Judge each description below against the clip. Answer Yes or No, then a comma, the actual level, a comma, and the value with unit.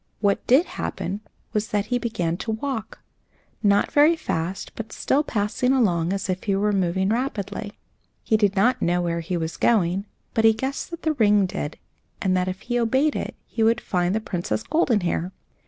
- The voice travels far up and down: No, average, 4.3 semitones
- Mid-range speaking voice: No, high, 210 Hz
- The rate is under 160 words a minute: No, average, 190 wpm